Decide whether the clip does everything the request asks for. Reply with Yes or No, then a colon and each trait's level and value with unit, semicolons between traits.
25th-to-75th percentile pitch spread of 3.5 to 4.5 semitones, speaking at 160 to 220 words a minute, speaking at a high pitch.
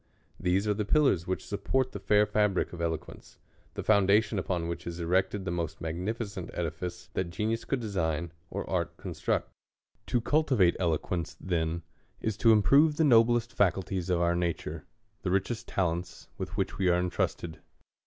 No: average, 4.0 semitones; average, 165 wpm; very low, 95 Hz